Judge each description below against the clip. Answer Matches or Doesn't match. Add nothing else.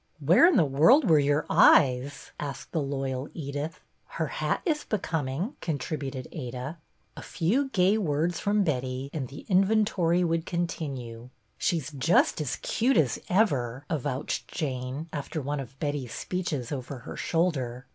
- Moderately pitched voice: Matches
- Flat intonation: Doesn't match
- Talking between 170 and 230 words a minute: Doesn't match